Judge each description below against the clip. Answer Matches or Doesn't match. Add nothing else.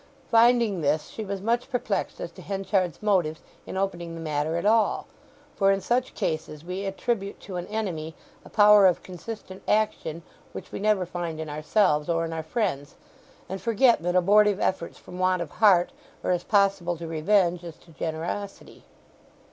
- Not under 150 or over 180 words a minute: Matches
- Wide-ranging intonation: Doesn't match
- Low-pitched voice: Doesn't match